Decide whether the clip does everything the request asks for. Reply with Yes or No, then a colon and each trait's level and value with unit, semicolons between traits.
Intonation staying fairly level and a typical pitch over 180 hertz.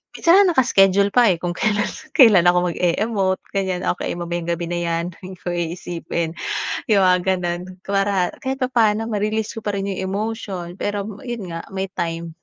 No: average, 3.4 semitones; high, 190 Hz